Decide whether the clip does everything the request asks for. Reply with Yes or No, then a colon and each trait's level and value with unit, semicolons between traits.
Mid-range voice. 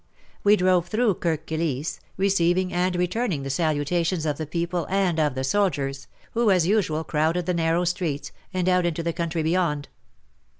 Yes: medium, 170 Hz